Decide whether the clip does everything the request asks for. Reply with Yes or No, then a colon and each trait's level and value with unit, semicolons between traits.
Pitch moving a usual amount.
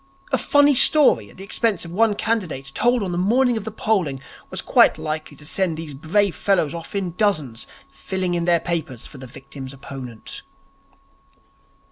No: wide, 6.6 semitones